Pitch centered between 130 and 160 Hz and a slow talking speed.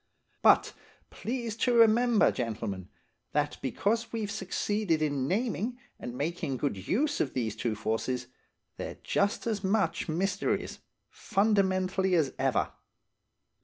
No: high, 190 Hz; slow, 120 wpm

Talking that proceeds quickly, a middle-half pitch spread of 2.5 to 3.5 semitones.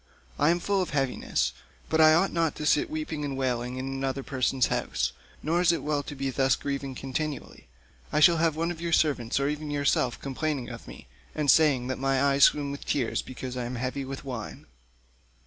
Yes: fast, 210 wpm; average, 3.1 semitones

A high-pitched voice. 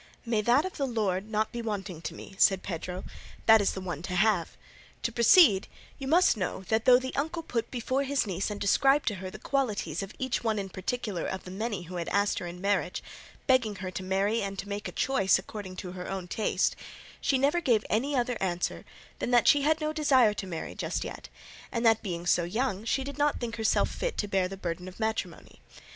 Yes: high, 215 Hz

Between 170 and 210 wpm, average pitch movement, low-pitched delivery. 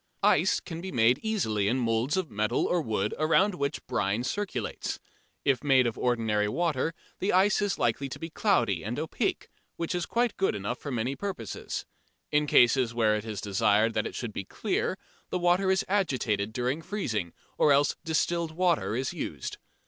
No: average, 180 wpm; wide, 7.7 semitones; low, 130 Hz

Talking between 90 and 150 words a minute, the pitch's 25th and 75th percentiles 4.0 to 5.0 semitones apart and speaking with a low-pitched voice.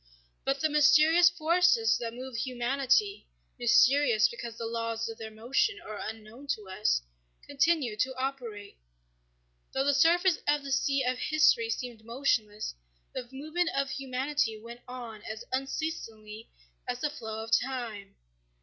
No: average, 140 wpm; average, 4.4 semitones; very high, 255 Hz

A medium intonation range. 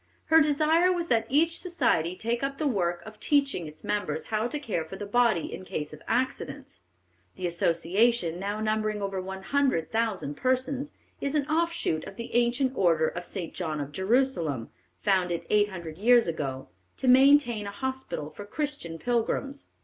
No: wide, 7.4 semitones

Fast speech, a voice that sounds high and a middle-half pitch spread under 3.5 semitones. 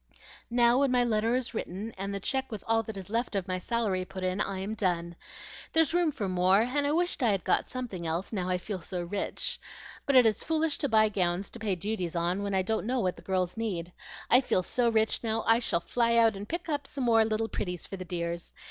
No: fast, 245 wpm; high, 215 Hz; average, 4.5 semitones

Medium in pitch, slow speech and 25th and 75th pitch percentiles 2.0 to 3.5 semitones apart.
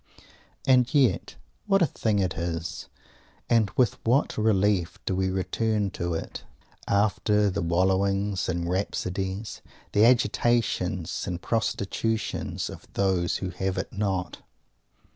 No: low, 100 Hz; slow, 125 wpm; average, 3.2 semitones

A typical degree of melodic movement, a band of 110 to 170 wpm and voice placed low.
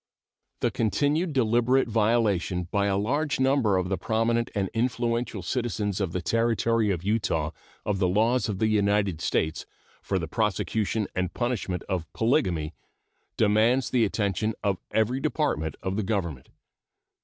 Yes: average, 3.7 semitones; average, 145 wpm; low, 110 Hz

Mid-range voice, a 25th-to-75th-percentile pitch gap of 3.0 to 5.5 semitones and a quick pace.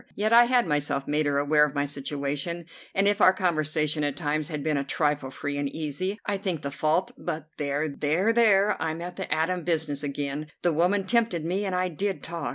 Yes: medium, 155 Hz; average, 4.2 semitones; fast, 215 wpm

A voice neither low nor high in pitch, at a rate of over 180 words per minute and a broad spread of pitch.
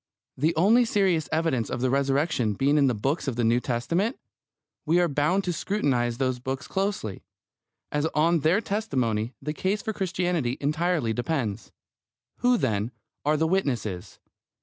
No: medium, 150 Hz; average, 155 wpm; wide, 6.4 semitones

